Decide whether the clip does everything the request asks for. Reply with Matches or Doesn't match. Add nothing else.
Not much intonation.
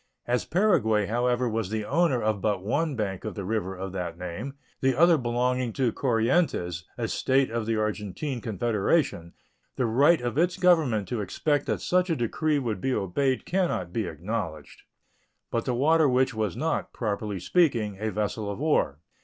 Doesn't match